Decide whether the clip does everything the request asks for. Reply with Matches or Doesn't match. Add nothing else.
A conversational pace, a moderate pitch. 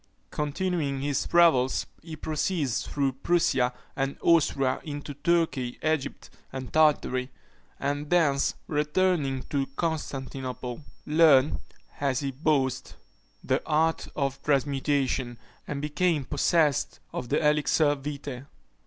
Doesn't match